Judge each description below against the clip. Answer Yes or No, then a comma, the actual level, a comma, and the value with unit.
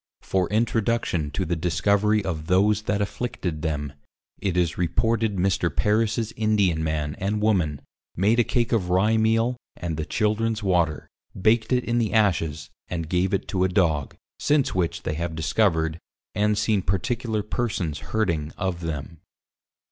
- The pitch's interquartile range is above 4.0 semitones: Yes, average, 4.8 semitones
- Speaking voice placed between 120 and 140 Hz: No, very low, 95 Hz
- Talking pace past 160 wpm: No, average, 155 wpm